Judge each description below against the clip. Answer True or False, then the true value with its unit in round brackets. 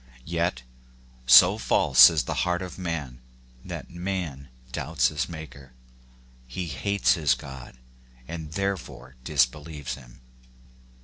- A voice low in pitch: True (75 Hz)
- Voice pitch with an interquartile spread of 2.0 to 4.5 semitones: False (5.0 semitones)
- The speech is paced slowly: True (120 wpm)